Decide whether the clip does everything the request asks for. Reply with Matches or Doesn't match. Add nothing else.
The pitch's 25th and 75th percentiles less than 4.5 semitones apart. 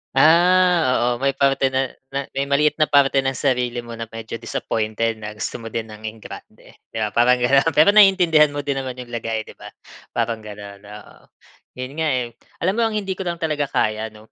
Doesn't match